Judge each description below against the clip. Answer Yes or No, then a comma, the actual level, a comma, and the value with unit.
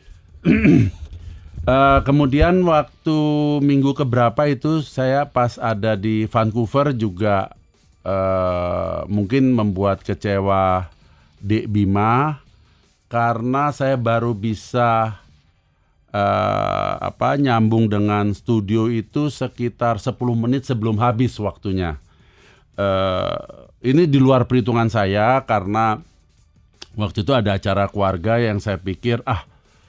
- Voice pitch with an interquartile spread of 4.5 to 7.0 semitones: Yes, average, 4.8 semitones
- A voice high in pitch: No, low, 110 Hz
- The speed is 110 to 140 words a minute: No, average, 100 wpm